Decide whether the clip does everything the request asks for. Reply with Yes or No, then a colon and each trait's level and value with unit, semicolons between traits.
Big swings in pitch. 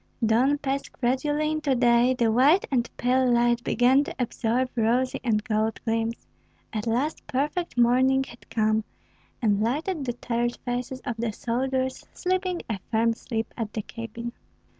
No: narrow, 2.6 semitones